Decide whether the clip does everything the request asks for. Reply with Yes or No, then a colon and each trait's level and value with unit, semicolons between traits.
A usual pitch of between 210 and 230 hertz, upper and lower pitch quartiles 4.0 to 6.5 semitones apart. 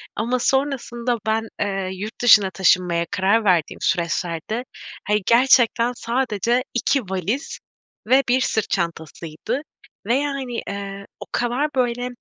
Yes: high, 225 Hz; average, 4.5 semitones